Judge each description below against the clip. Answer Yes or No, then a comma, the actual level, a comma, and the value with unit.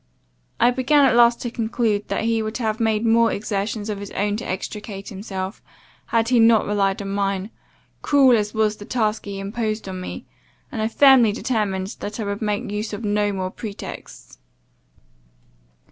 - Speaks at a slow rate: No, average, 175 wpm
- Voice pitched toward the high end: Yes, high, 215 Hz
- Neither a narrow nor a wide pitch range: No, narrow, 2.3 semitones